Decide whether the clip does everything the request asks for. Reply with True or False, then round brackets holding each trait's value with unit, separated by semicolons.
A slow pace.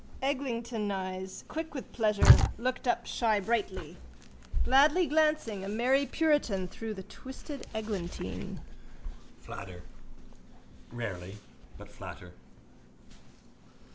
True (85 wpm)